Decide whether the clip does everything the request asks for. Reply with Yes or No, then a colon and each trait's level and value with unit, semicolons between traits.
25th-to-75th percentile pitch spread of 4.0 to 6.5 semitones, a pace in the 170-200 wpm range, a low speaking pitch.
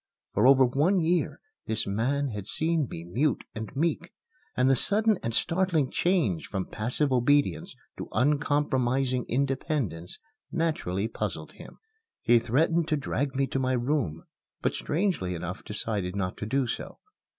No: wide, 5.6 semitones; average, 150 wpm; low, 130 Hz